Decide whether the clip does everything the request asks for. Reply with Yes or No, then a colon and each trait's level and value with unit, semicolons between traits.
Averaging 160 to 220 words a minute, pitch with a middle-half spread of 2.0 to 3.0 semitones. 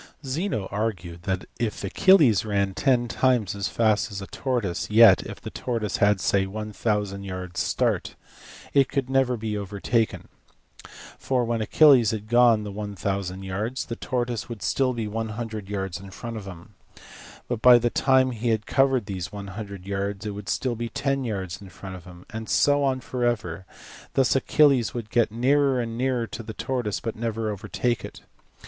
No: average, 175 wpm; average, 3.7 semitones